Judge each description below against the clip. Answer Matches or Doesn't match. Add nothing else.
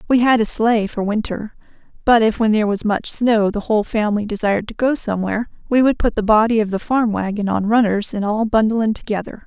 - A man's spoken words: Doesn't match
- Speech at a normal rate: Doesn't match